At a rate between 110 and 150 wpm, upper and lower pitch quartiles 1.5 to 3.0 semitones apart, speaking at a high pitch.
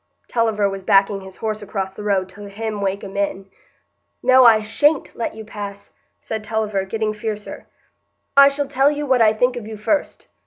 No: average, 185 wpm; narrow, 2.5 semitones; high, 215 Hz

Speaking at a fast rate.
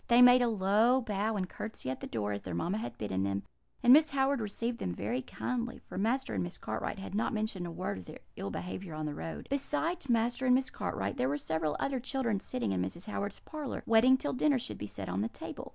Yes: fast, 245 wpm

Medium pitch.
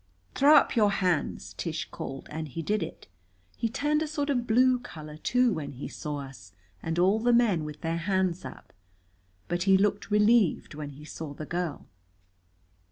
Yes: medium, 180 Hz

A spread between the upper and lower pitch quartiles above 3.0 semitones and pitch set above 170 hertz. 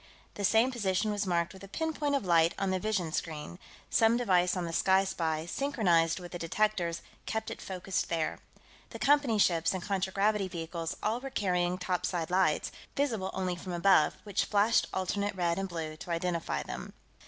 Yes: average, 3.5 semitones; medium, 185 Hz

